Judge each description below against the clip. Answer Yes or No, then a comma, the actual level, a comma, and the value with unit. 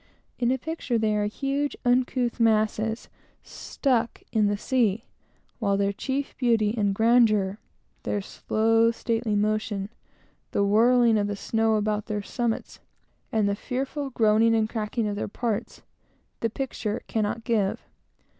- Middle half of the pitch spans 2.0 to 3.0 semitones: Yes, narrow, 2.4 semitones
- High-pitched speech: Yes, high, 225 Hz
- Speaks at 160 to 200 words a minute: No, average, 140 wpm